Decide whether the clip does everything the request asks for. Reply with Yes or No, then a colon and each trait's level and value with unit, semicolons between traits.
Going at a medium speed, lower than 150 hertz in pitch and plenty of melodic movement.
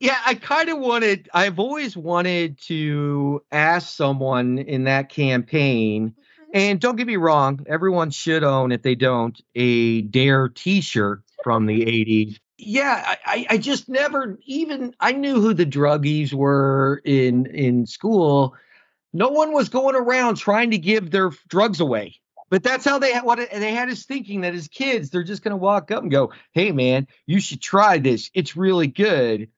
No: average, 175 wpm; medium, 175 Hz; wide, 8.5 semitones